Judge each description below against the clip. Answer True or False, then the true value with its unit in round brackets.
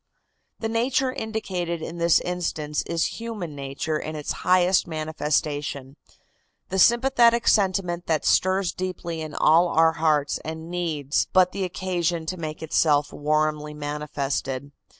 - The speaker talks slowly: True (130 wpm)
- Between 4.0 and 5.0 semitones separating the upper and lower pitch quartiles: False (3.5 semitones)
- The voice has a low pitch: False (165 Hz)